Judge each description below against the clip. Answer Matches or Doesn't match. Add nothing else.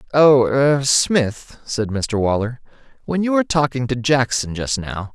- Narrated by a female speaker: Doesn't match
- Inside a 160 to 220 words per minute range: Doesn't match